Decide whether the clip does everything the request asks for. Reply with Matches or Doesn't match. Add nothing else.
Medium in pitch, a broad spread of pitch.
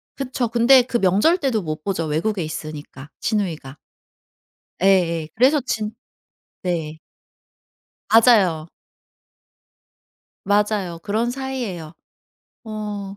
Doesn't match